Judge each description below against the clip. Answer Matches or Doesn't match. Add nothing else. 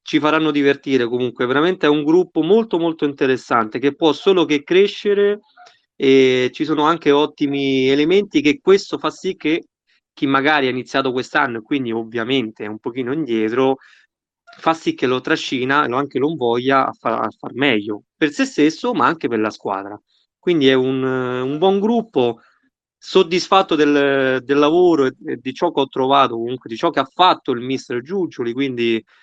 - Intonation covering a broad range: Doesn't match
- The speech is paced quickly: Matches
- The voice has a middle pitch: Matches